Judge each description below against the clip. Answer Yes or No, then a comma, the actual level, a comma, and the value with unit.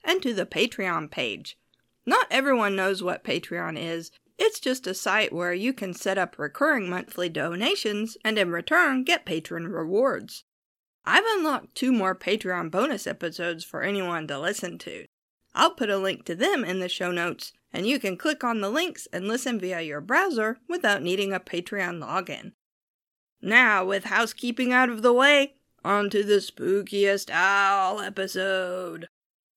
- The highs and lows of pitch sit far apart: Yes, wide, 5.7 semitones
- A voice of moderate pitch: No, high, 200 Hz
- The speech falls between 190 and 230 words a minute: No, average, 165 wpm